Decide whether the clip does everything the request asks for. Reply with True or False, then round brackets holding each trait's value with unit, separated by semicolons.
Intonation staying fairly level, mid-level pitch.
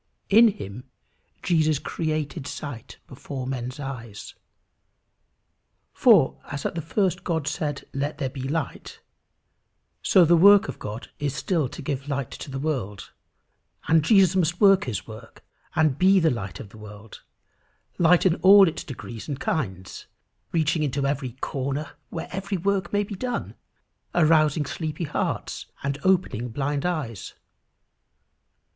False (4.8 semitones; 150 Hz)